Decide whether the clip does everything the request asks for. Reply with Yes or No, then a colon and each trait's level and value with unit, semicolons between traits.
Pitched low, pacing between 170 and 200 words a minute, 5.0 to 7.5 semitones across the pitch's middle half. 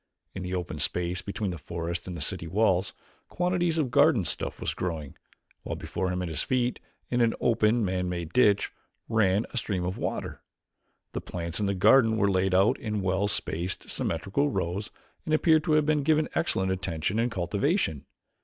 Yes: low, 100 Hz; average, 185 wpm; wide, 5.4 semitones